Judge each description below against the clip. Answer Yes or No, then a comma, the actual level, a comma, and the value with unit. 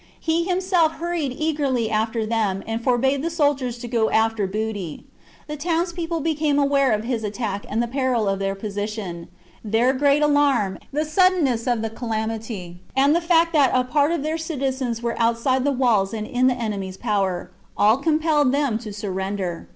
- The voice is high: Yes, high, 245 Hz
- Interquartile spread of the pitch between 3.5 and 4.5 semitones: No, average, 5.3 semitones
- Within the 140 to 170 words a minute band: No, average, 180 wpm